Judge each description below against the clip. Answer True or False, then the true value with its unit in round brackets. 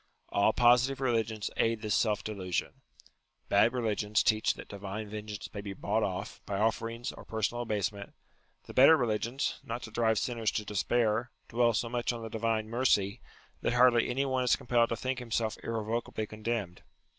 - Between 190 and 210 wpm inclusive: False (170 wpm)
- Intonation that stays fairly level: True (2.1 semitones)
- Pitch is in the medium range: False (115 Hz)